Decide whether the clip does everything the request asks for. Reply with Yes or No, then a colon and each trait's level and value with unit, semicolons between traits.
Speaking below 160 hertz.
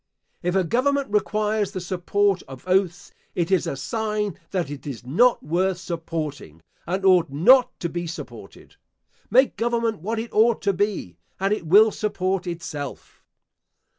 No: high, 190 Hz